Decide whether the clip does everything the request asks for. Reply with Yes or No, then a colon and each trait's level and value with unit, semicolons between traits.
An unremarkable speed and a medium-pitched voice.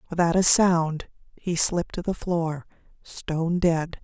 Yes: average, 150 wpm; medium, 170 Hz